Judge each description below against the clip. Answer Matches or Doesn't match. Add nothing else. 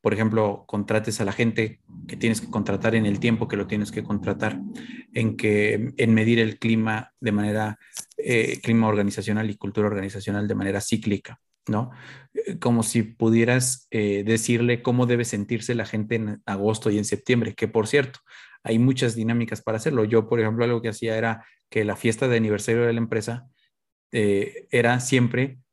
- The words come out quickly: Doesn't match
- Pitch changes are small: Matches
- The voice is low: Matches